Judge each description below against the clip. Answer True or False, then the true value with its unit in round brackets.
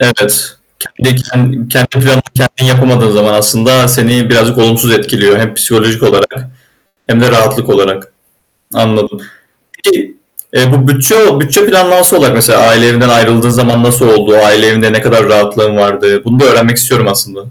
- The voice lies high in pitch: False (120 Hz)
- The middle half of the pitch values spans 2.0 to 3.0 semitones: True (2.7 semitones)